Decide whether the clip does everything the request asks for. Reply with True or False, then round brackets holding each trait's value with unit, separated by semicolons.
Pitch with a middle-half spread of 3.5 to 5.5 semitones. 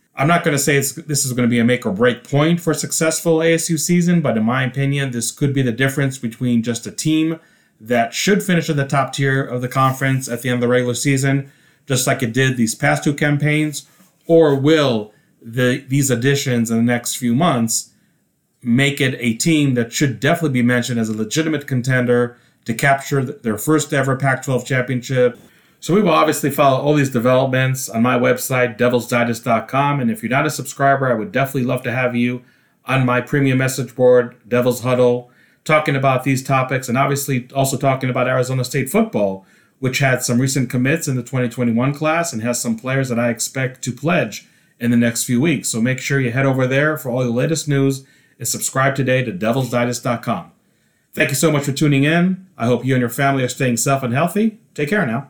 False (2.6 semitones)